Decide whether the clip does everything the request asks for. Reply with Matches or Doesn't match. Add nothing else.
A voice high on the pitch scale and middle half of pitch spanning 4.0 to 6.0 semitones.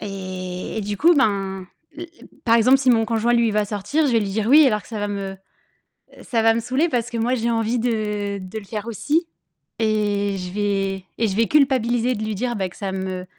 Doesn't match